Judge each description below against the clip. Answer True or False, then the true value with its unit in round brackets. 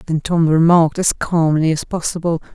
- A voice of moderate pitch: True (165 Hz)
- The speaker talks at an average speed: True (165 wpm)